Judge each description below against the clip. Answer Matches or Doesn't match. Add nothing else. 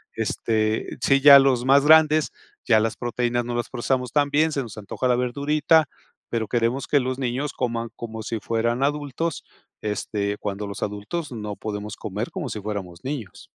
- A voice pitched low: Matches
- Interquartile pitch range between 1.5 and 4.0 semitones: Doesn't match